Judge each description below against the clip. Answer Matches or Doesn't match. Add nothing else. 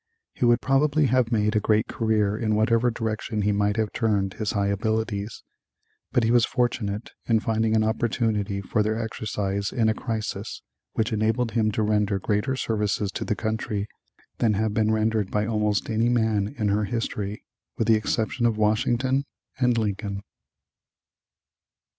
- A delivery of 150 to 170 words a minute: Matches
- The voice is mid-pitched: Doesn't match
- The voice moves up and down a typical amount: Doesn't match